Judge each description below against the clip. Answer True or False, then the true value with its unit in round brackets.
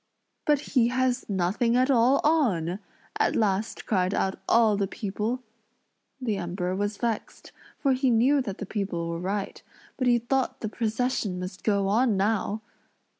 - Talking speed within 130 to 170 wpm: True (160 wpm)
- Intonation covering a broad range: False (4.3 semitones)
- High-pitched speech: True (215 Hz)